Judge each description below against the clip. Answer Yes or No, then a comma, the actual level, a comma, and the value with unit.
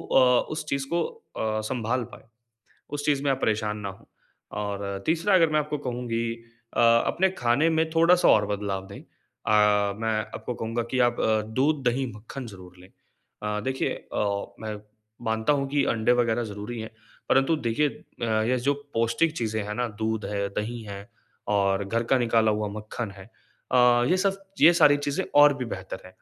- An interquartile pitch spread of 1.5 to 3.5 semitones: No, average, 4.7 semitones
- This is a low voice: Yes, low, 115 Hz